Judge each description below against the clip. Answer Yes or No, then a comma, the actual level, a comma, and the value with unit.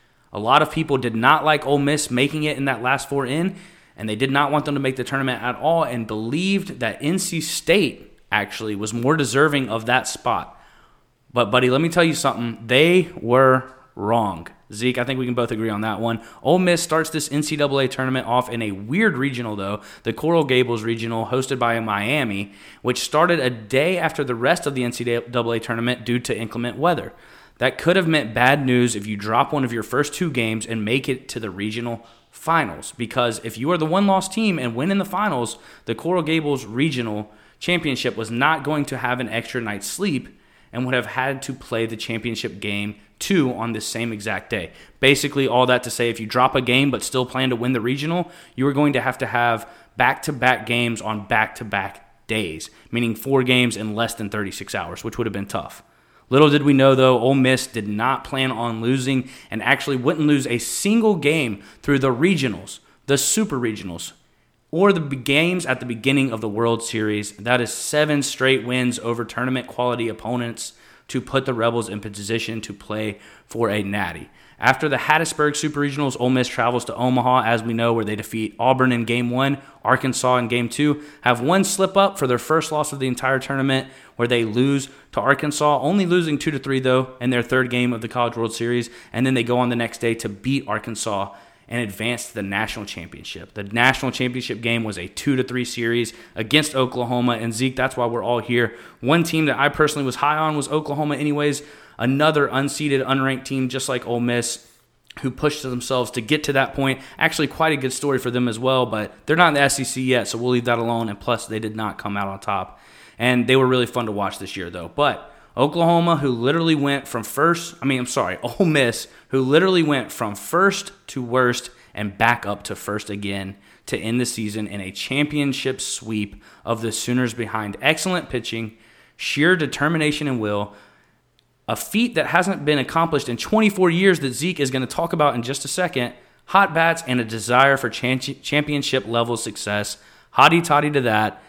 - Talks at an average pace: No, fast, 210 wpm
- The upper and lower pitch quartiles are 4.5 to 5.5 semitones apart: No, average, 3.9 semitones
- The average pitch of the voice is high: No, low, 125 Hz